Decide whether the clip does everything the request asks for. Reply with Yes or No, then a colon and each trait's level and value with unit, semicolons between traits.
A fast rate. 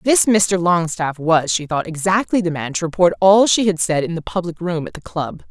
Yes: fast, 240 wpm